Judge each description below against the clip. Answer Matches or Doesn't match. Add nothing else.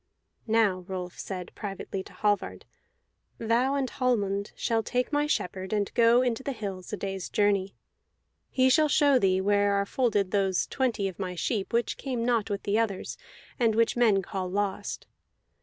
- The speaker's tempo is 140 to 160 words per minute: Doesn't match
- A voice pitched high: Matches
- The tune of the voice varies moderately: Matches